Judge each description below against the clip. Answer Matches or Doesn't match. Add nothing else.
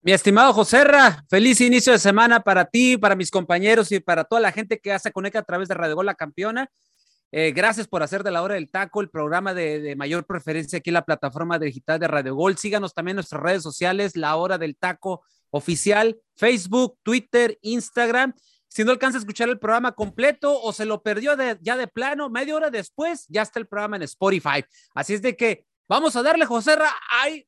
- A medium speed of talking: Doesn't match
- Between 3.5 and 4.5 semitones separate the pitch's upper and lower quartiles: Doesn't match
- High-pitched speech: Matches